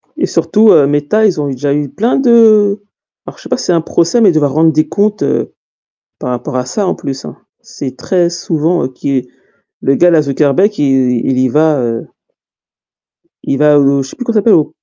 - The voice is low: No, medium, 155 Hz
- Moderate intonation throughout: No, wide, 6.7 semitones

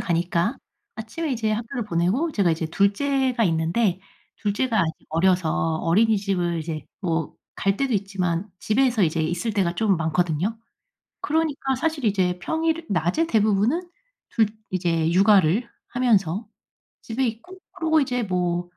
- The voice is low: No, high, 200 Hz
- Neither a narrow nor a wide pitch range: No, wide, 6.0 semitones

